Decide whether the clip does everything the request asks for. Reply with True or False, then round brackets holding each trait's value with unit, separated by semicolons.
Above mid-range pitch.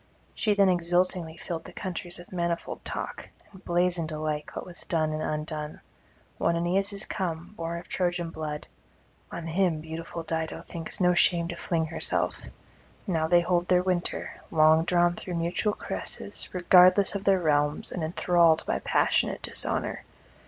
False (170 Hz)